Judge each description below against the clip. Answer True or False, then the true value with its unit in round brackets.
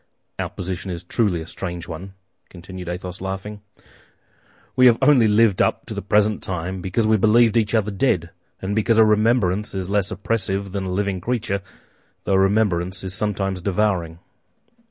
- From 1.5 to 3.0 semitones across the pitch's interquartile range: True (2.7 semitones)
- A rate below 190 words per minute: True (170 wpm)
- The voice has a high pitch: False (95 Hz)